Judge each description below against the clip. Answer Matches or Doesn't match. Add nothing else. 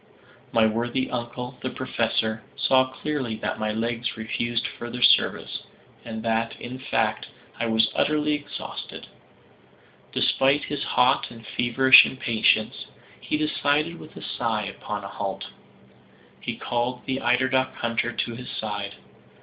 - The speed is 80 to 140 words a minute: Matches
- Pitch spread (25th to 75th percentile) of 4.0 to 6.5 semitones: Doesn't match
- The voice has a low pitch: Matches